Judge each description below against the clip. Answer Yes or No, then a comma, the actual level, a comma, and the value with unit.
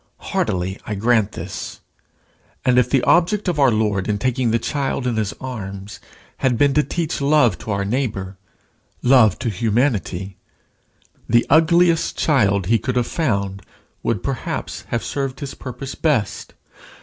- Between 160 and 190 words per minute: No, average, 150 wpm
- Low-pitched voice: Yes, low, 120 Hz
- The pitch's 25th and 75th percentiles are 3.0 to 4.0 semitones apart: No, average, 5.3 semitones